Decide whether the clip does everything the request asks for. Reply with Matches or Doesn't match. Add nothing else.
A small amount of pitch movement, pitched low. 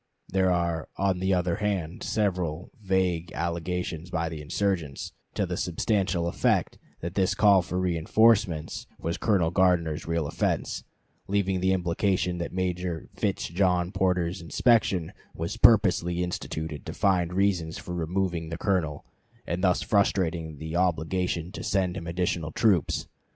Matches